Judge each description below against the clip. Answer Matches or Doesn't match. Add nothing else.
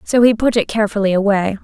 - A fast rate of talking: Matches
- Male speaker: Doesn't match